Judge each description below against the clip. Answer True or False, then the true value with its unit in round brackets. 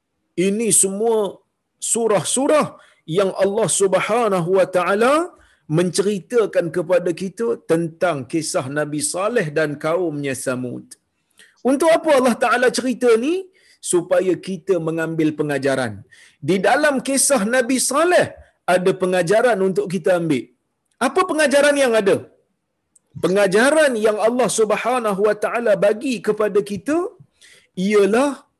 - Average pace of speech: True (110 wpm)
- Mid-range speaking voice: False (205 Hz)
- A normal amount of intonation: False (6.2 semitones)